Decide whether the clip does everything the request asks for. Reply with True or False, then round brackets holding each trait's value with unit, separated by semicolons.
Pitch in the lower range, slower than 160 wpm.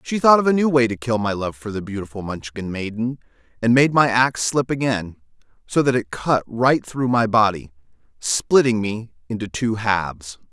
False (115 Hz; 195 wpm)